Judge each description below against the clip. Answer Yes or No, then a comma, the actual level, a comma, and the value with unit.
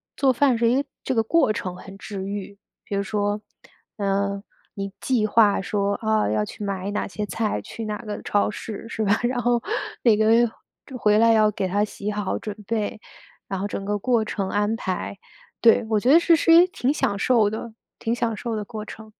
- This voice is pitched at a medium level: No, high, 210 Hz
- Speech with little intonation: Yes, narrow, 2.3 semitones